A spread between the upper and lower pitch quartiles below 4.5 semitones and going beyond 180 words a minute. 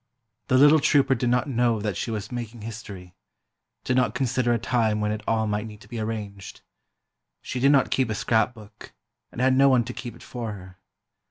Yes: average, 3.0 semitones; average, 200 wpm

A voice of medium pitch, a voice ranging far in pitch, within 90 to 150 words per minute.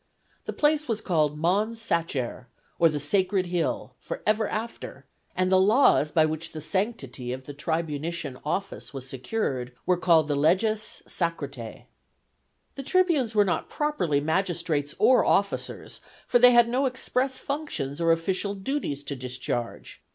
Yes: medium, 175 Hz; wide, 7.2 semitones; average, 145 wpm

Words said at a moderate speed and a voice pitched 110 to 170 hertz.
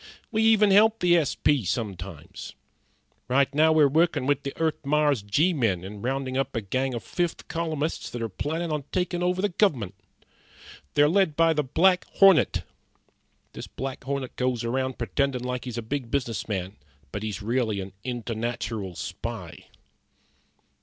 Yes: average, 160 wpm; low, 135 Hz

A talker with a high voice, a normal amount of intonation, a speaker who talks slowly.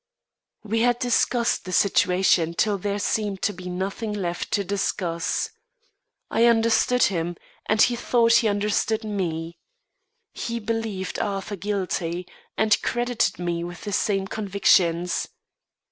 Yes: high, 200 Hz; average, 3.7 semitones; slow, 130 wpm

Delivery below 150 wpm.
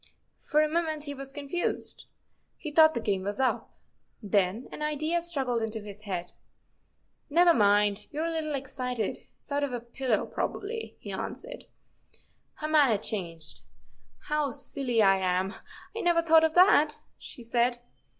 No: average, 170 wpm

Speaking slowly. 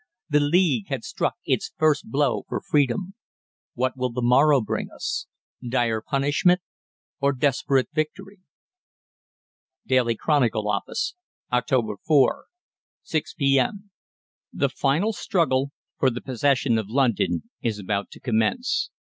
Yes: slow, 120 wpm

